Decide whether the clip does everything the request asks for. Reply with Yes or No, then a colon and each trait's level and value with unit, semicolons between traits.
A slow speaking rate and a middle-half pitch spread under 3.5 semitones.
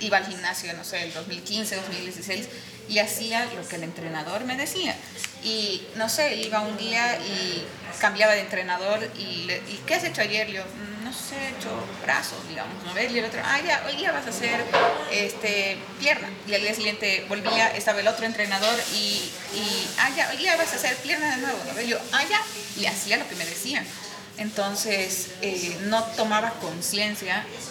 No: average, 190 wpm; average, 3.0 semitones